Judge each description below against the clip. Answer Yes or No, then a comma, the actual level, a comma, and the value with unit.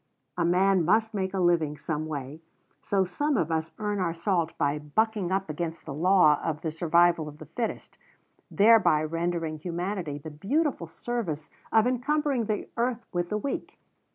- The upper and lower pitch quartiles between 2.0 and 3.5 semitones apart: No, average, 5.1 semitones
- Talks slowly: No, average, 170 wpm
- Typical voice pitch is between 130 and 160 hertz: No, medium, 175 Hz